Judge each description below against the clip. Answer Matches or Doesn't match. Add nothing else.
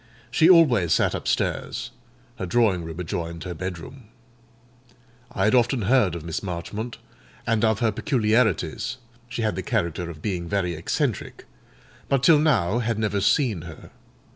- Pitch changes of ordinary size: Doesn't match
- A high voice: Doesn't match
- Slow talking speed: Doesn't match